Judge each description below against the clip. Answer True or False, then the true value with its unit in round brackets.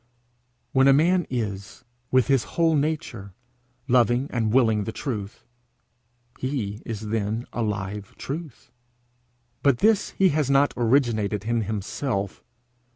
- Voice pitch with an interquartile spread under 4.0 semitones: False (4.8 semitones)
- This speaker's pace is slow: True (125 wpm)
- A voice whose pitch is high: False (120 Hz)